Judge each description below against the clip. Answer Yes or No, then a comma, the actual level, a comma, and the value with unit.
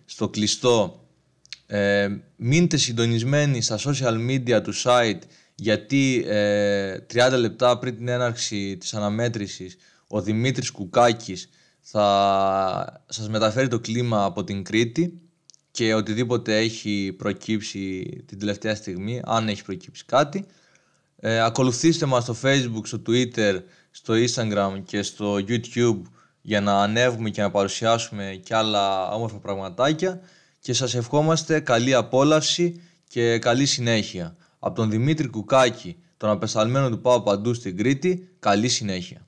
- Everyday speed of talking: Yes, average, 130 wpm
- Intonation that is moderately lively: Yes, average, 3.8 semitones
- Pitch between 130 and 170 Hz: No, low, 115 Hz